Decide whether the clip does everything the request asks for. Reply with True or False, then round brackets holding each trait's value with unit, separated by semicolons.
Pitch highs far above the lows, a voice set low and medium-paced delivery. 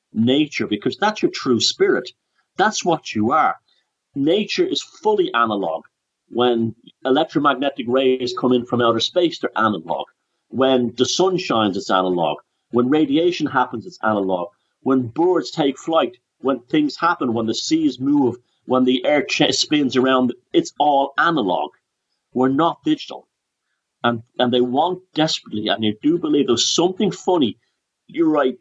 True (6.9 semitones; 130 Hz; 150 wpm)